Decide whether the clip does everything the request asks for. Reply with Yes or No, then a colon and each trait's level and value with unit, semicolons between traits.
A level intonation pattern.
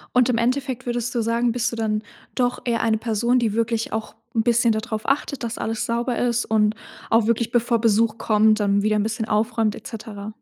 Yes: narrow, 1.6 semitones